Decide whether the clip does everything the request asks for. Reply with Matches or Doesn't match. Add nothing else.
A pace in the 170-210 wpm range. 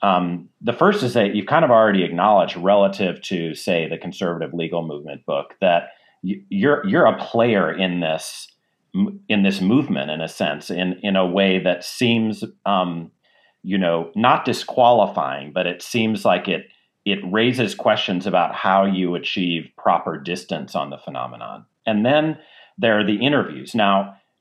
Doesn't match